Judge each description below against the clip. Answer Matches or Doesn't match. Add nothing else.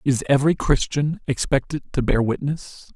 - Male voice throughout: Matches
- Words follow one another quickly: Doesn't match